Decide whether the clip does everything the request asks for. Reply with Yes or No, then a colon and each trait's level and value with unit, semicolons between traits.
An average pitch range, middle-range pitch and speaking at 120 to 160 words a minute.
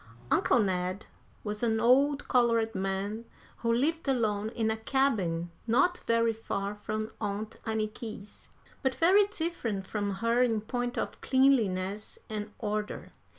No: average, 3.1 semitones; high, 220 Hz; slow, 135 wpm